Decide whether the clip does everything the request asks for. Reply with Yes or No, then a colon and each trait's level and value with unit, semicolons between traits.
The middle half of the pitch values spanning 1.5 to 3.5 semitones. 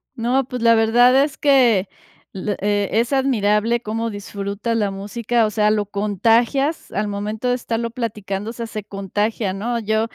Yes: narrow, 2.5 semitones